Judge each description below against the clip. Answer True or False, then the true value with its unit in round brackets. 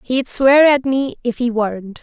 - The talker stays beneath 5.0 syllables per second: True (4.4 syllables/s)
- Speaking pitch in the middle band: False (250 Hz)